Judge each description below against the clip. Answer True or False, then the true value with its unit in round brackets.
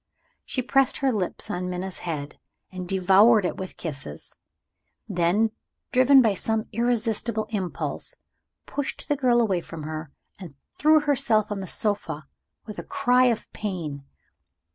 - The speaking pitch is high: True (210 Hz)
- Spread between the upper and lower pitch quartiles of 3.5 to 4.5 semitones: False (5.1 semitones)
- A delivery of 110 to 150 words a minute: True (140 wpm)